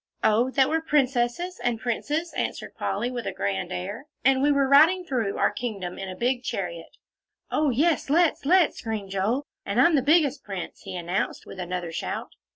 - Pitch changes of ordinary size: No, wide, 7.0 semitones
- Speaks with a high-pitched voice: Yes, high, 245 Hz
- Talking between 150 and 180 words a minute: No, average, 190 wpm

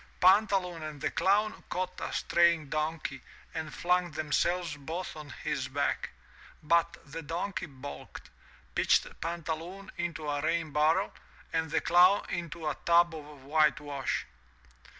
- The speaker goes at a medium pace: No, slow, 130 wpm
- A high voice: No, medium, 165 Hz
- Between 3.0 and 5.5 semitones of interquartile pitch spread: No, narrow, 2.5 semitones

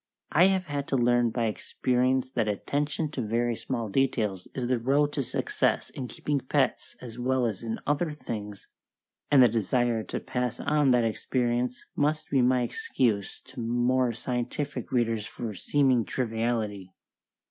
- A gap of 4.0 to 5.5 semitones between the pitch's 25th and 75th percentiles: No, average, 2.8 semitones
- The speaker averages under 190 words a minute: Yes, average, 160 wpm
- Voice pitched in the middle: No, low, 125 Hz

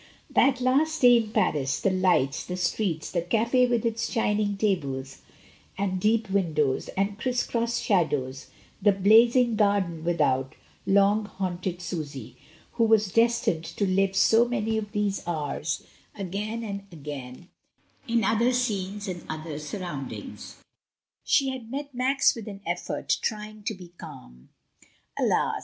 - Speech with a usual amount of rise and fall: Yes, average, 4.9 semitones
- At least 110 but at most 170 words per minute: Yes, average, 140 wpm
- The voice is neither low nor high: No, high, 200 Hz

